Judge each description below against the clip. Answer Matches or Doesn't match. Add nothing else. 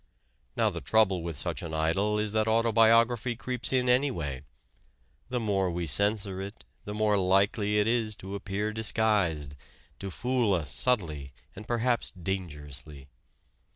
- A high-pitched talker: Doesn't match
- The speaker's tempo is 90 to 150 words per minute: Matches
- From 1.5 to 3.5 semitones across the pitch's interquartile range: Doesn't match